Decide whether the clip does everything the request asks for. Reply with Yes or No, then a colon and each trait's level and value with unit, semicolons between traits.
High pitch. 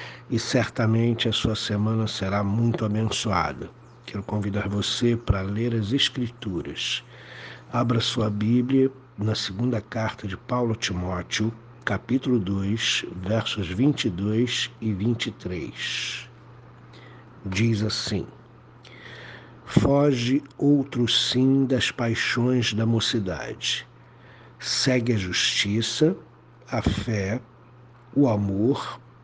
No: low, 115 Hz